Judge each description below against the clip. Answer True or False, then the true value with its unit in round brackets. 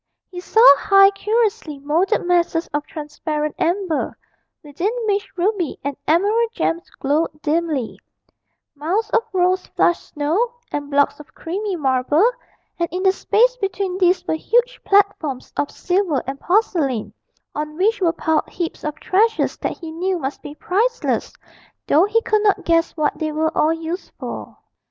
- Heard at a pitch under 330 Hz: False (345 Hz)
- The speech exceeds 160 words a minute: False (155 wpm)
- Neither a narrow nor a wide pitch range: True (4.7 semitones)